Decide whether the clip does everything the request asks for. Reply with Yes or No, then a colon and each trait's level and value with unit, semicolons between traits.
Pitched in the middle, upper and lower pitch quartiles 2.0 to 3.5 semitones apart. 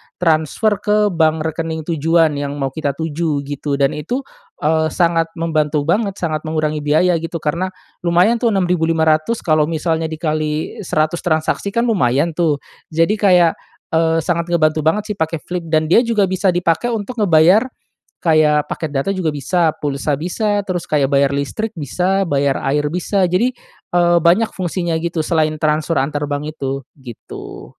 Yes: medium, 160 Hz; average, 2.8 semitones